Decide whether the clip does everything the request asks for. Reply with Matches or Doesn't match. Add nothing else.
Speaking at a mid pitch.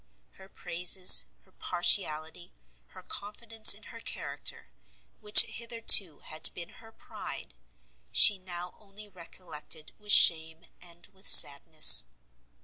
Matches